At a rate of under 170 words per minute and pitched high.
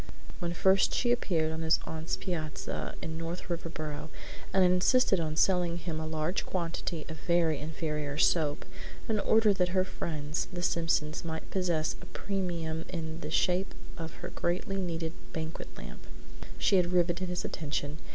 No: average, 160 wpm; medium, 165 Hz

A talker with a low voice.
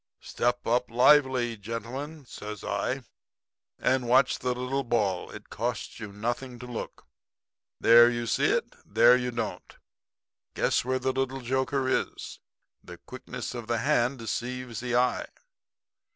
Yes: low, 120 Hz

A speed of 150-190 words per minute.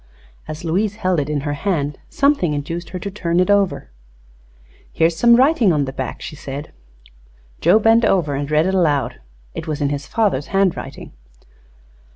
Yes: average, 180 wpm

